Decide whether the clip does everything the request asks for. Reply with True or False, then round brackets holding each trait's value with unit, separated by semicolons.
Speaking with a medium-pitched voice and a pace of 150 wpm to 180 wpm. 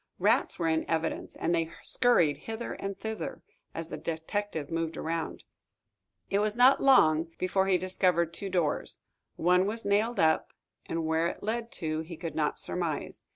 True (170 Hz; 165 wpm)